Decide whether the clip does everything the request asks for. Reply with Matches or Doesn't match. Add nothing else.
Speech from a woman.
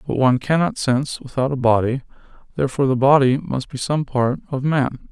Doesn't match